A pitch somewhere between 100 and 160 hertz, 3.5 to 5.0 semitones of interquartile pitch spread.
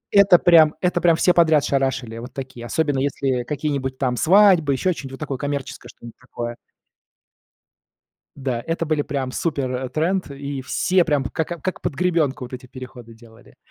Yes: medium, 140 Hz; average, 4.2 semitones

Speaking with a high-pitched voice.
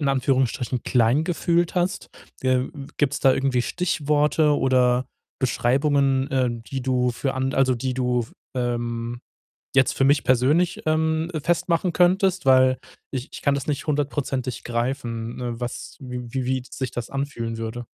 No: low, 130 Hz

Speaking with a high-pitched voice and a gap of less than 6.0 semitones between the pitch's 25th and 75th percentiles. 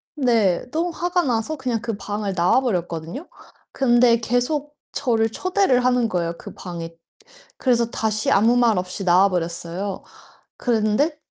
Yes: high, 230 Hz; average, 5.1 semitones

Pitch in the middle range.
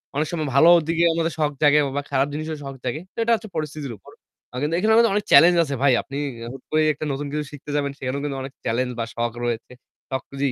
Yes: medium, 145 Hz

